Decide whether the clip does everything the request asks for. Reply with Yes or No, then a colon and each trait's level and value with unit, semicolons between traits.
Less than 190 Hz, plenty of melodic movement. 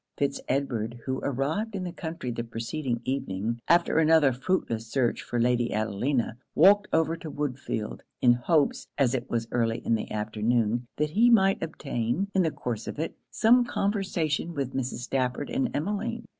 Yes: low, 135 Hz; wide, 6.0 semitones